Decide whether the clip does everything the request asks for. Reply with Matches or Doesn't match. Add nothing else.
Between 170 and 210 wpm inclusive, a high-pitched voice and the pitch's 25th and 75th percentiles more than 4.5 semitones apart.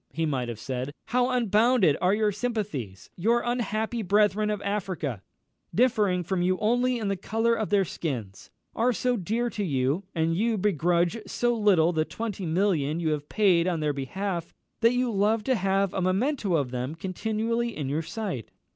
Matches